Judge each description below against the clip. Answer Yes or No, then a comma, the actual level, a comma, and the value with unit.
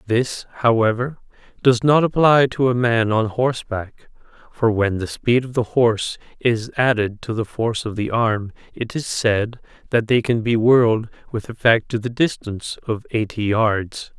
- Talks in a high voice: No, low, 115 Hz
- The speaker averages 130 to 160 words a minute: No, average, 175 wpm